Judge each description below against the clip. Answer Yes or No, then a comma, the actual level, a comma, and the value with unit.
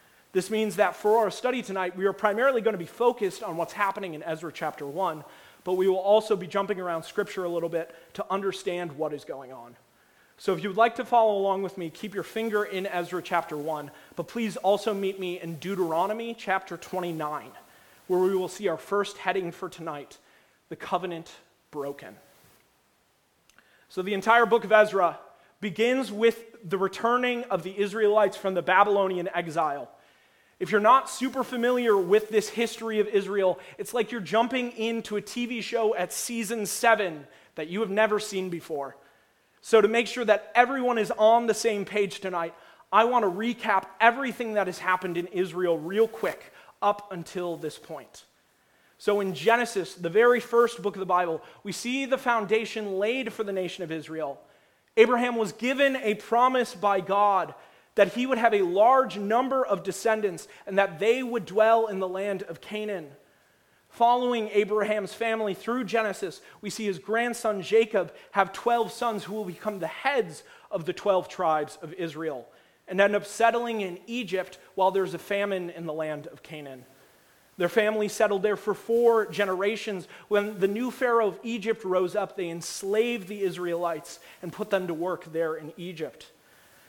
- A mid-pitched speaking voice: No, high, 200 Hz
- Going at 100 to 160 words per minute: No, average, 180 wpm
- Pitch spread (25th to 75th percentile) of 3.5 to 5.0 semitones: Yes, average, 3.8 semitones